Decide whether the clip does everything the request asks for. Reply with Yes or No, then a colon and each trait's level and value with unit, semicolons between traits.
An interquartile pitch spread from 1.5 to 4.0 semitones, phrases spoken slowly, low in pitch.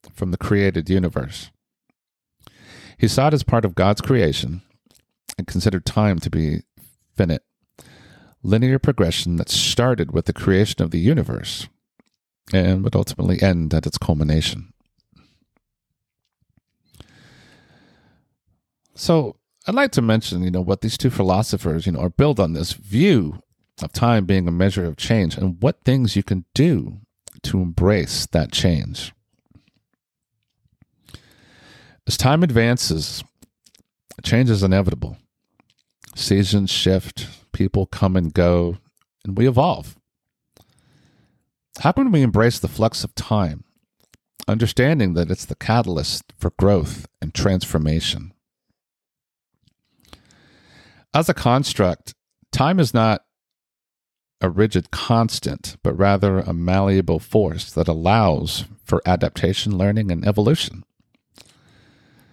No: average, 4.5 semitones; slow, 120 wpm; low, 100 Hz